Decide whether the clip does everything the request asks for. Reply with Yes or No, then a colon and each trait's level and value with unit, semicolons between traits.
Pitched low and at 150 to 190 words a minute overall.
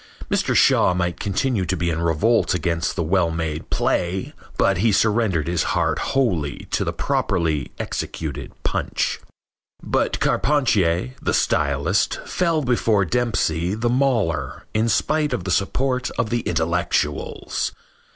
No: very low, 90 Hz; slow, 135 wpm